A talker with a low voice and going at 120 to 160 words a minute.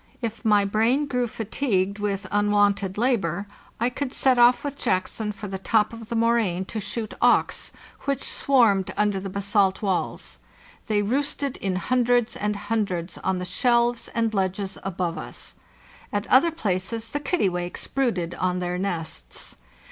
No: high, 210 Hz; average, 155 wpm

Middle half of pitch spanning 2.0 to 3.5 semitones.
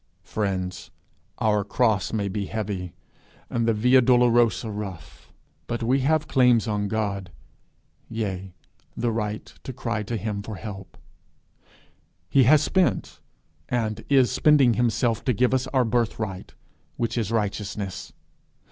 Yes: average, 3.2 semitones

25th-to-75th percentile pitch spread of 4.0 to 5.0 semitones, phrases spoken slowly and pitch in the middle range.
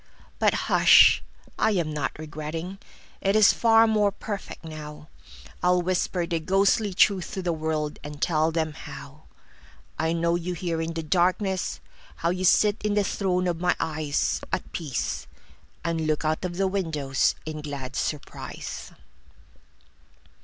No: average, 3.5 semitones; slow, 130 wpm; medium, 165 Hz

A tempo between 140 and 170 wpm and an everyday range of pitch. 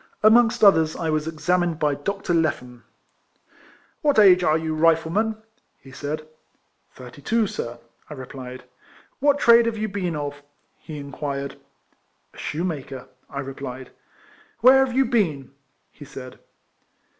No: average, 155 wpm; wide, 6.8 semitones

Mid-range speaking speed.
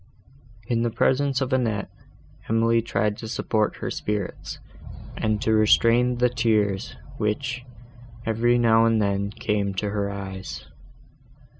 No: slow, 130 wpm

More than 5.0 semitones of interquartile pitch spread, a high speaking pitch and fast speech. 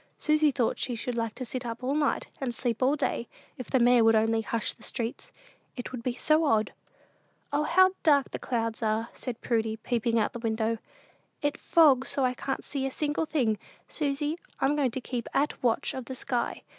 No: average, 3.6 semitones; very high, 250 Hz; fast, 210 wpm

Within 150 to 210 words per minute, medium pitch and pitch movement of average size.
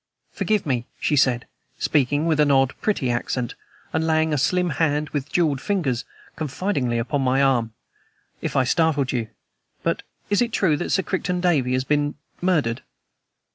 Yes: average, 165 wpm; medium, 145 Hz; average, 4.2 semitones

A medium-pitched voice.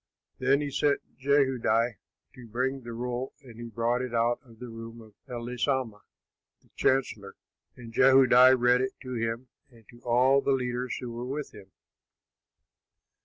No: low, 125 Hz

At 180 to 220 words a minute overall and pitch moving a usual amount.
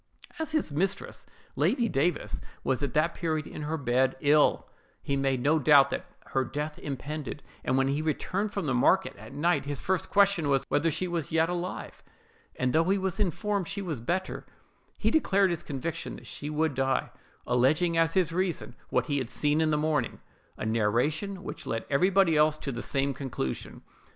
Yes: average, 185 wpm; average, 4.5 semitones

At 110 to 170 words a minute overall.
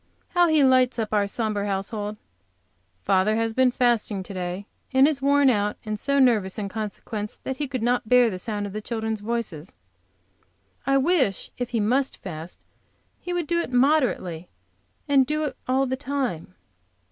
No: average, 180 wpm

